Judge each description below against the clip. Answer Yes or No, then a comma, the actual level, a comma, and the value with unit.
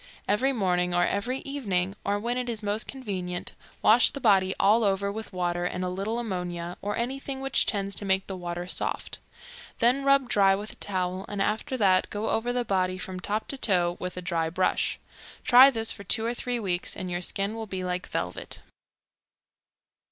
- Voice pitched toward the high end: Yes, high, 200 Hz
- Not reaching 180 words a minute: No, average, 195 wpm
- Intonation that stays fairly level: No, average, 4.0 semitones